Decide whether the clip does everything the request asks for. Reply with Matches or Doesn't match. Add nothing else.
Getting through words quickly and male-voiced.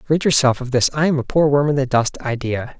Matches